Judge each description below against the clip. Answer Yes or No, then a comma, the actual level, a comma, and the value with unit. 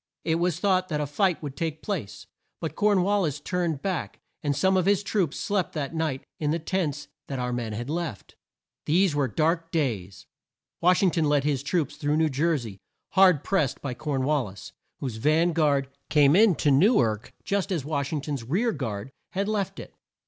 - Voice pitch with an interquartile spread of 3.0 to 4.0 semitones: No, average, 4.7 semitones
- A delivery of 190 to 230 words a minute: Yes, fast, 205 wpm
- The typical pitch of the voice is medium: Yes, medium, 155 Hz